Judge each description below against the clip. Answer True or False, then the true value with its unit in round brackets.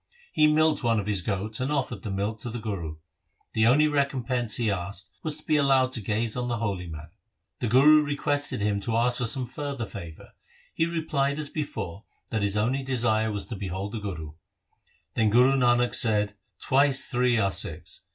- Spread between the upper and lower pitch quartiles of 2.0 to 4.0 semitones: False (4.9 semitones)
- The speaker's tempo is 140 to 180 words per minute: False (195 wpm)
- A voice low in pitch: True (120 Hz)